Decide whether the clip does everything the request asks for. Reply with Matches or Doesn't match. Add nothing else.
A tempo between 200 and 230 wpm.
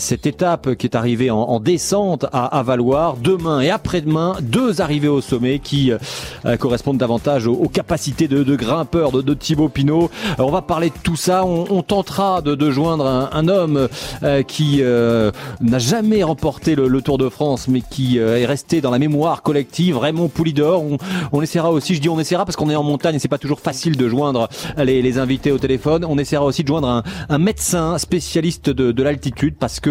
Matches